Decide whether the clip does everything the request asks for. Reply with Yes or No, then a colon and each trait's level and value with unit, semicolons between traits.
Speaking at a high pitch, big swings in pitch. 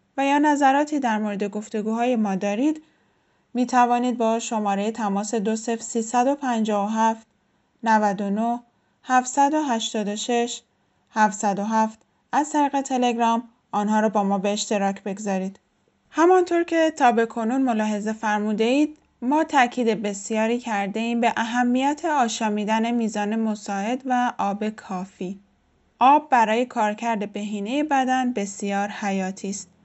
No: high, 225 Hz; average, 3.1 semitones